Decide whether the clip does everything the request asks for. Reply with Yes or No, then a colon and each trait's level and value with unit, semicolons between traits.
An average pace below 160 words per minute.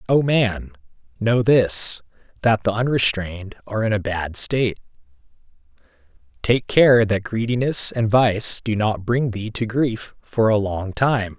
Yes: average, 150 wpm